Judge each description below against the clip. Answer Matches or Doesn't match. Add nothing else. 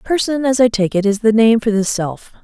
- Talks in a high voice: Matches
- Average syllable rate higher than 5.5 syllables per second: Doesn't match